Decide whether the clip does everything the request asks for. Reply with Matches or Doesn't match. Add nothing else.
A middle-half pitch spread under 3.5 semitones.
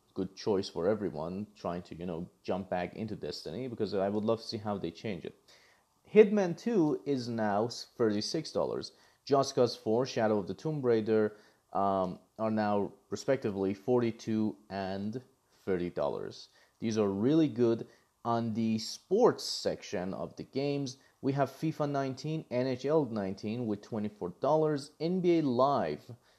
Doesn't match